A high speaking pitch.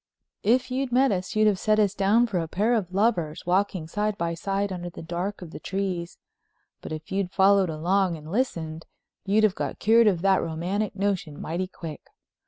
Yes: high, 195 Hz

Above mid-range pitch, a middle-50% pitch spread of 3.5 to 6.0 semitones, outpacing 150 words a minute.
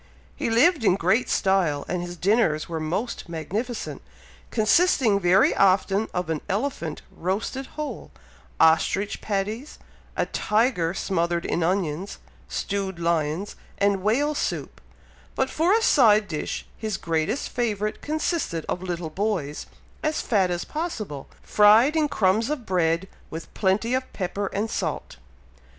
No: high, 200 Hz; average, 5.1 semitones; slow, 135 wpm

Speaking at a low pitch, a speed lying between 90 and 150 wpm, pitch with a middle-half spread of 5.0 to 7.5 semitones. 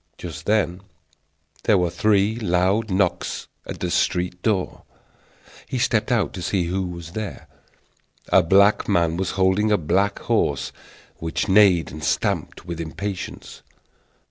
No: very low, 95 Hz; average, 140 wpm; average, 3.0 semitones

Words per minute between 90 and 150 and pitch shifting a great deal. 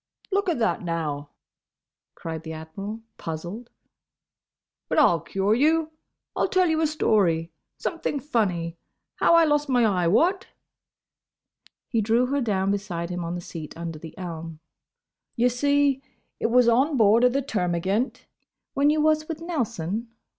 Yes: average, 145 wpm; wide, 8.9 semitones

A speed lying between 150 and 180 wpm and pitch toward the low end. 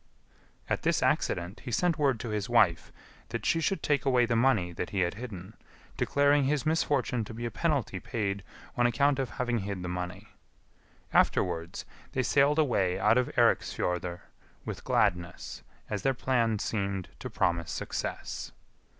Yes: average, 160 wpm; low, 115 Hz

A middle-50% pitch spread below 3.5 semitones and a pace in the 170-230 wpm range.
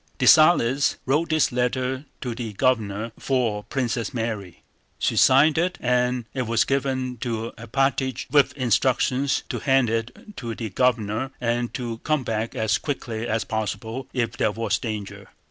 No: average, 2.8 semitones; average, 150 wpm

